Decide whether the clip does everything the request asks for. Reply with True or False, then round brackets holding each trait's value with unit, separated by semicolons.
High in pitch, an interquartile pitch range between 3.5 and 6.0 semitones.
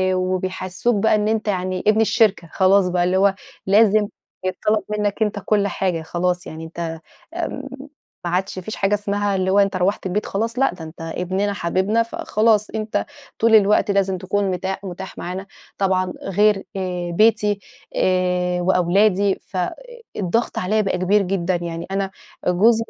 False (195 Hz; 2.4 semitones)